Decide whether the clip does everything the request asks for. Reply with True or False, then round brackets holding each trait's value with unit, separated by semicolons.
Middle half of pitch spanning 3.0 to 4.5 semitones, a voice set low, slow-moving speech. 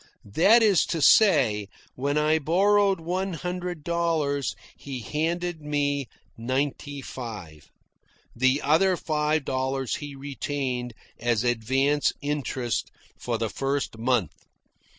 False (4.2 semitones; 145 Hz; 110 wpm)